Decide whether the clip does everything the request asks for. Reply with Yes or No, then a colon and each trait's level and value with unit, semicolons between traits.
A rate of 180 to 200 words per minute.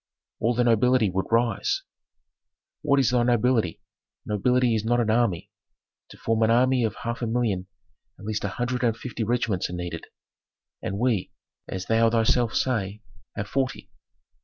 No: average, 160 wpm